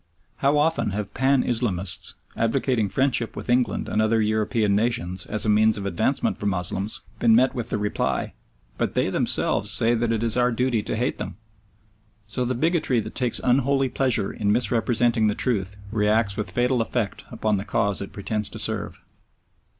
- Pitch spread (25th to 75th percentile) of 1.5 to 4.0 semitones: Yes, average, 3.0 semitones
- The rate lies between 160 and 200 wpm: Yes, average, 180 wpm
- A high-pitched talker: No, low, 115 Hz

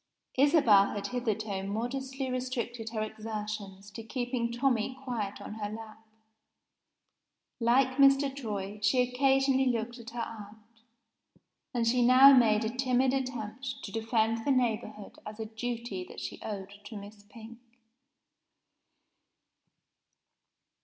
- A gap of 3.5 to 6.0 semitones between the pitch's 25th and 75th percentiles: No, average, 3.0 semitones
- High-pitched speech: Yes, high, 230 Hz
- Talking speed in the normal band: No, slow, 125 wpm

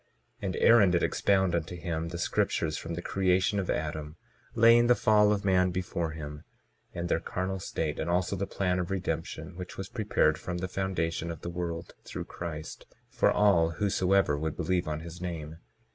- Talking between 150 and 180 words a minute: No, average, 190 wpm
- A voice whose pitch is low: Yes, very low, 90 Hz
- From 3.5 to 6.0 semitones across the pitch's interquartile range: No, average, 2.7 semitones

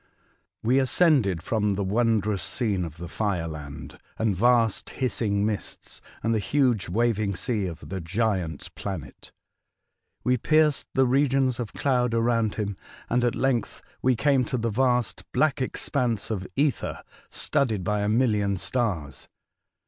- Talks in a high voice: No, low, 110 Hz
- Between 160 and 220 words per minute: No, average, 145 wpm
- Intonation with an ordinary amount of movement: Yes, average, 4.3 semitones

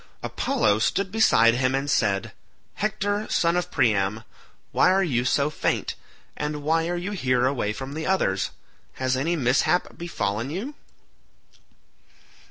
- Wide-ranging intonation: Yes, wide, 6.7 semitones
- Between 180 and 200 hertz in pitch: No, medium, 145 Hz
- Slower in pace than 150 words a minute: Yes, average, 140 wpm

